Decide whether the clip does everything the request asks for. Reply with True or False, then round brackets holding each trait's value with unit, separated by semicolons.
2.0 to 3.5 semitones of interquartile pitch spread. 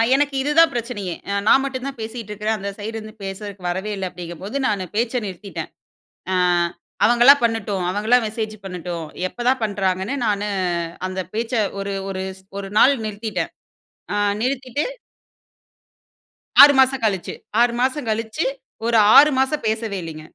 False (4.2 semitones)